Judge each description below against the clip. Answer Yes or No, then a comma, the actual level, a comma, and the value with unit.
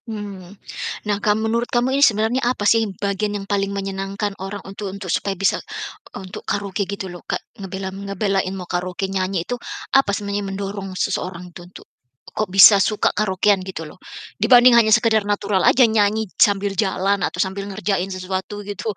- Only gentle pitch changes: Yes, narrow, 1.7 semitones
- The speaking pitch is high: Yes, high, 200 Hz